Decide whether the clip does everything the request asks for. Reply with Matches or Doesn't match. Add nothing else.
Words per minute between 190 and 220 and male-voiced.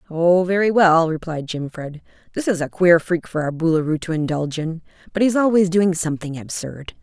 Doesn't match